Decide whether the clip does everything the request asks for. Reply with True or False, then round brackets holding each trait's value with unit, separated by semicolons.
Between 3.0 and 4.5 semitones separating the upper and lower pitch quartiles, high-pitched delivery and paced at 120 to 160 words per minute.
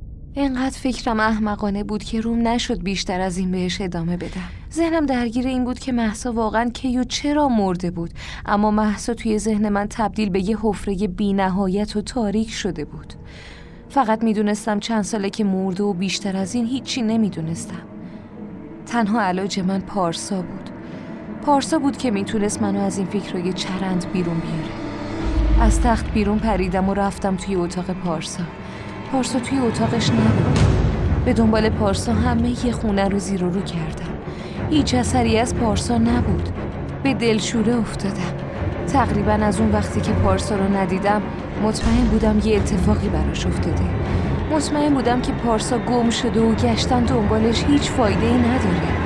True (3.5 semitones; 205 Hz; 155 wpm)